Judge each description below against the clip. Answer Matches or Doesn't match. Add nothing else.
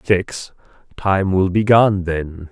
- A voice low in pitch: Matches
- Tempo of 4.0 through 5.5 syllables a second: Doesn't match